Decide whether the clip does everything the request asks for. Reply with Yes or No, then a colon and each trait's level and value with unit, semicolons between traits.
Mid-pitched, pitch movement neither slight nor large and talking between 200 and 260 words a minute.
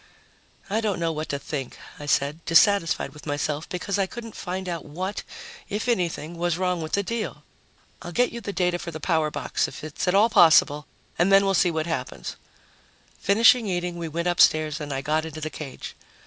Yes: medium, 170 Hz; average, 3.9 semitones; fast, 205 wpm